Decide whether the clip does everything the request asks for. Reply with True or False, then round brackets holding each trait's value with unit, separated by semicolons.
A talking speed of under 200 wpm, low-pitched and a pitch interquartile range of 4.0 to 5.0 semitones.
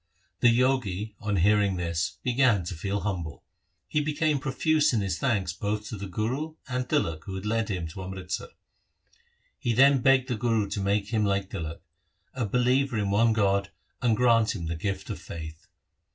True (185 wpm; 105 Hz; 4.6 semitones)